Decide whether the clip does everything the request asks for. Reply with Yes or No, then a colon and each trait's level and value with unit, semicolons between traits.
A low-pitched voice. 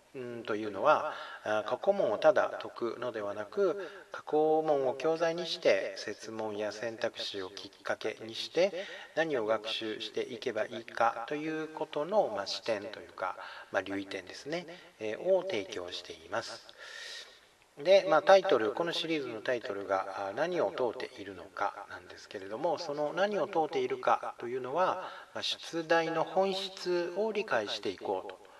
No: medium, 155 Hz